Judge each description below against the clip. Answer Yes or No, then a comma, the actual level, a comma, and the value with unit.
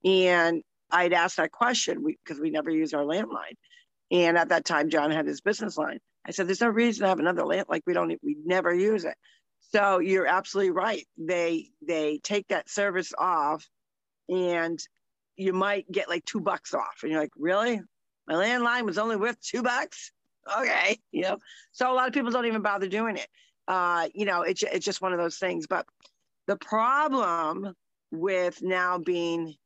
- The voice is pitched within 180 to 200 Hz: Yes, high, 190 Hz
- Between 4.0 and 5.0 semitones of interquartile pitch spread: Yes, average, 4.3 semitones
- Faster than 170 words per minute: Yes, average, 195 wpm